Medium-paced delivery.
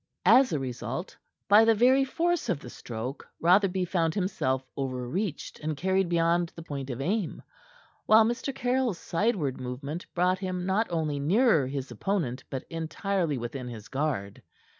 Yes: average, 160 wpm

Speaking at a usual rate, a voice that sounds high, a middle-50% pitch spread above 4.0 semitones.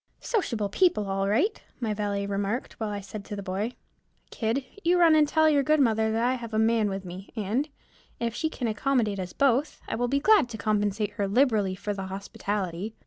No: fast, 210 wpm; high, 220 Hz; average, 4.5 semitones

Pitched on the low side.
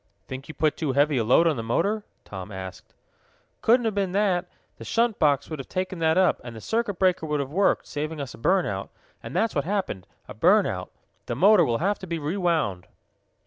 No: medium, 160 Hz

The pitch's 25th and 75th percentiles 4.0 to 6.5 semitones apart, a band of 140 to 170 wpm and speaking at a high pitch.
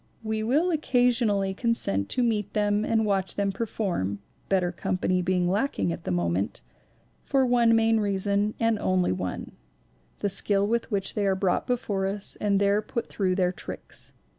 No: average, 3.3 semitones; average, 165 wpm; high, 200 Hz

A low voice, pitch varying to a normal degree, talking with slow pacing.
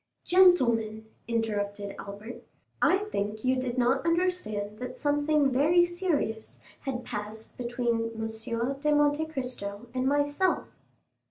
No: very high, 250 Hz; average, 4.9 semitones; slow, 115 wpm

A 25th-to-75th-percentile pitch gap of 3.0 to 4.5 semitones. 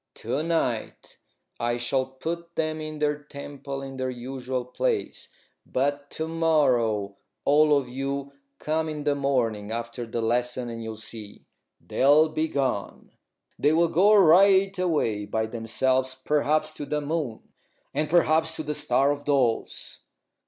Yes: average, 4.1 semitones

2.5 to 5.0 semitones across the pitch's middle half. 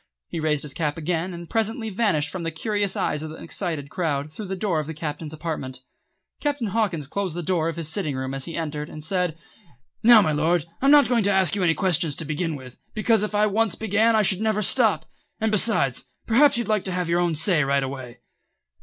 No: wide, 5.5 semitones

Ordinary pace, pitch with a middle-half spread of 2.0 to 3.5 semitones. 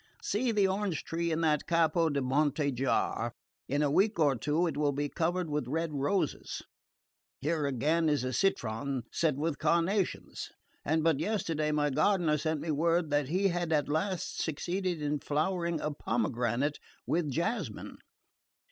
Yes: average, 160 wpm; average, 3.0 semitones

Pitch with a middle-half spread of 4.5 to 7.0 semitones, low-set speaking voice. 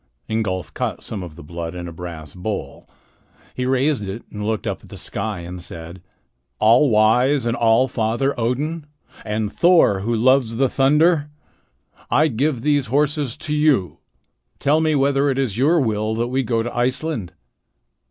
Yes: average, 5.1 semitones; low, 120 Hz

